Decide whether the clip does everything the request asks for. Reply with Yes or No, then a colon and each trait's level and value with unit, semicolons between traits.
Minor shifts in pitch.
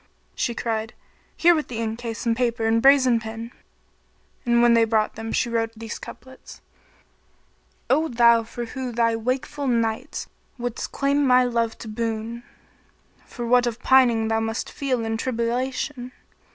Yes: narrow, 2.0 semitones